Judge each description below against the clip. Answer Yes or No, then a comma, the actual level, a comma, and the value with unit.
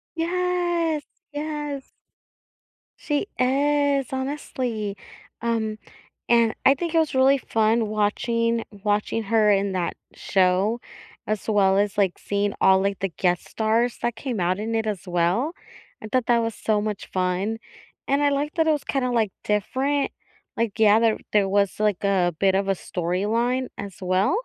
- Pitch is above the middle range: Yes, high, 220 Hz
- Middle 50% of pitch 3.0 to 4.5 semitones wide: No, average, 4.9 semitones